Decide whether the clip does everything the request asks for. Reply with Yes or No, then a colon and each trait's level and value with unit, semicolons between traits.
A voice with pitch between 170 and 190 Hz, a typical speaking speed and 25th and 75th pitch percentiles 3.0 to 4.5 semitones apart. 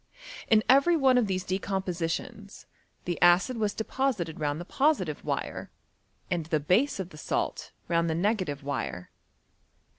No: medium, 185 Hz; average, 145 wpm; average, 5.1 semitones